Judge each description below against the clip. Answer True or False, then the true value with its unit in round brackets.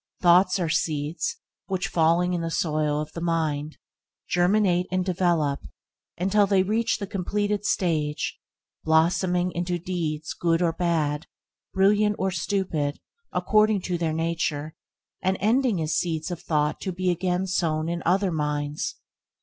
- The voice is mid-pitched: True (175 Hz)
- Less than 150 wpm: True (140 wpm)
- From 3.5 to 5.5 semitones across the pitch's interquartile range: False (3.0 semitones)